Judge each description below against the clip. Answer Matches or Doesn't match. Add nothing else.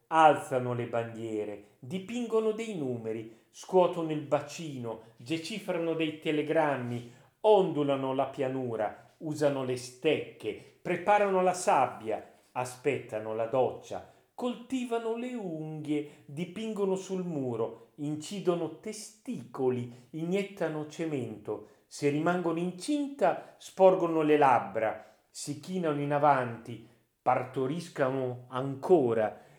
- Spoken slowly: Matches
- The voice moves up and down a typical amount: Doesn't match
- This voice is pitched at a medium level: Matches